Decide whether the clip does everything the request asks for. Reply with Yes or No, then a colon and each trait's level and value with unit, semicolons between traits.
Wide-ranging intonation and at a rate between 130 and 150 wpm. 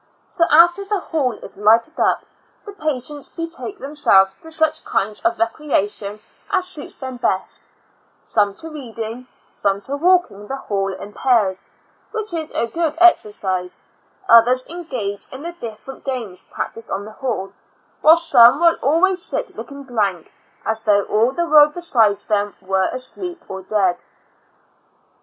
No: wide, 7.8 semitones; average, 160 wpm